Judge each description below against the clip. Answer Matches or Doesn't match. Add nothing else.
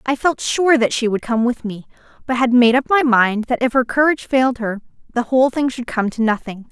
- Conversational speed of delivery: Doesn't match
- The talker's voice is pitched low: Doesn't match